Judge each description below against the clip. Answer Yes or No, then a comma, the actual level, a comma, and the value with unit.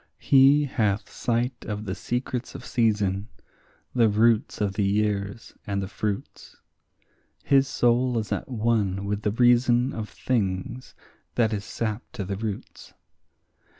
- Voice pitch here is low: Yes, low, 110 Hz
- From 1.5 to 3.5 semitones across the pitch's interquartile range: Yes, average, 3.2 semitones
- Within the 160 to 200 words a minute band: No, average, 140 wpm